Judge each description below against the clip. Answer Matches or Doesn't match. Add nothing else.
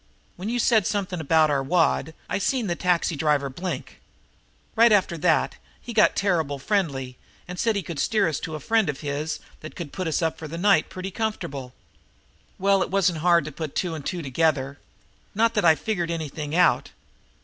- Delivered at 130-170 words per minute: Doesn't match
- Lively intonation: Doesn't match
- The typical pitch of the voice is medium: Matches